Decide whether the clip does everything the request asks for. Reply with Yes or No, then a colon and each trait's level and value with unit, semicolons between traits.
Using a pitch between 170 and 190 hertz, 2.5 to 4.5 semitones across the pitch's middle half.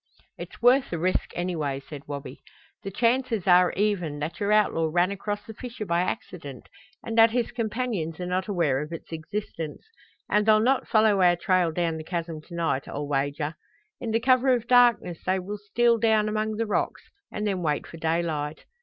No: medium, 185 Hz; average, 5.1 semitones